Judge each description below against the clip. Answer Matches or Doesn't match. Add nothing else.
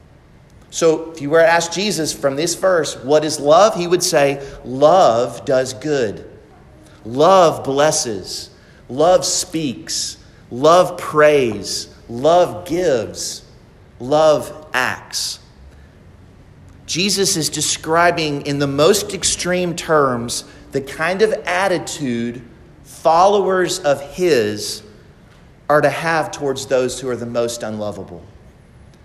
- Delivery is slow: Matches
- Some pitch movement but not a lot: Matches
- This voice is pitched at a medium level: Matches